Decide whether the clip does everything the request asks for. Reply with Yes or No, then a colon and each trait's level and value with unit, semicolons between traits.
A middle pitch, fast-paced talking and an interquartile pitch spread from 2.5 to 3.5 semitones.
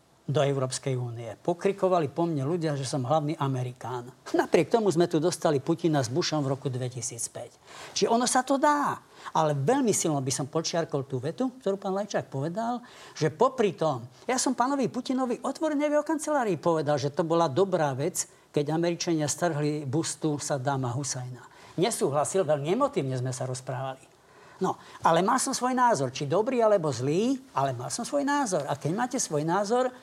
No: medium, 165 Hz; fast, 175 wpm; wide, 7.5 semitones